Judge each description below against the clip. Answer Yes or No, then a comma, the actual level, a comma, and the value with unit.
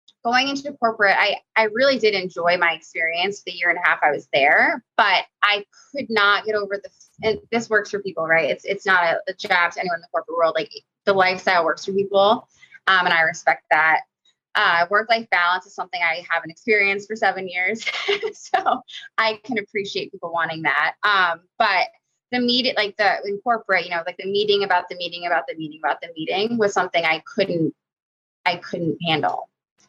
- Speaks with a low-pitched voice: No, high, 200 Hz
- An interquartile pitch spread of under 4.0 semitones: No, average, 4.4 semitones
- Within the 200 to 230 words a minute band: Yes, fast, 205 wpm